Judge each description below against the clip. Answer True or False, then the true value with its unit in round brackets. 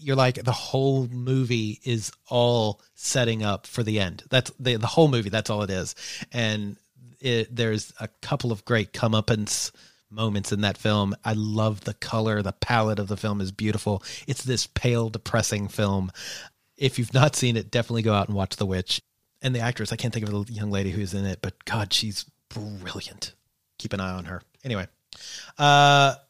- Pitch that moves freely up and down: False (3.1 semitones)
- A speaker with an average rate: True (195 wpm)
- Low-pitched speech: True (110 Hz)